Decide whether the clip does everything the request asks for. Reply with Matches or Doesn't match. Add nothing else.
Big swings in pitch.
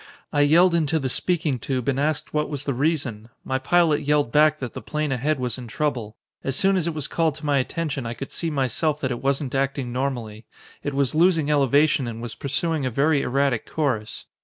Doesn't match